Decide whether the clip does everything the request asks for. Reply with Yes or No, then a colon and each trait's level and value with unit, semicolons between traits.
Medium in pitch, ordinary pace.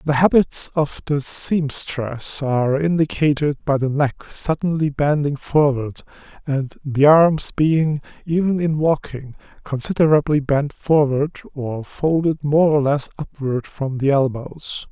No: medium, 145 Hz; slow, 130 wpm